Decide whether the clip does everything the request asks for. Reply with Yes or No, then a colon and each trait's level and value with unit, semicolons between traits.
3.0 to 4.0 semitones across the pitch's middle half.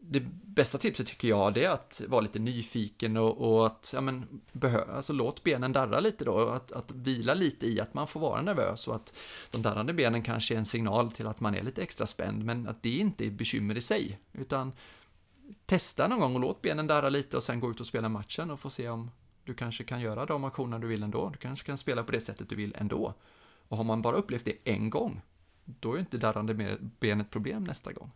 Yes: average, 3.5 semitones